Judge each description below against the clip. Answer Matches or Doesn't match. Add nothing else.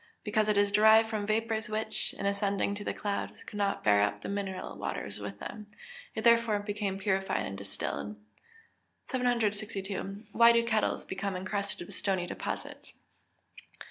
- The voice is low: Doesn't match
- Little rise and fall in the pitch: Matches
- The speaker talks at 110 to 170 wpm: Matches